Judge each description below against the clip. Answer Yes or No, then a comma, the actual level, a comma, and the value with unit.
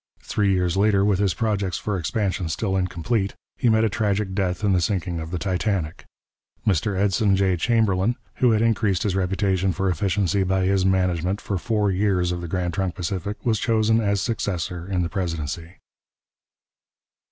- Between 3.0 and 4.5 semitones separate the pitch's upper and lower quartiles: No, narrow, 2.4 semitones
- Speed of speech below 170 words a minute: No, average, 175 wpm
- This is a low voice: Yes, very low, 95 Hz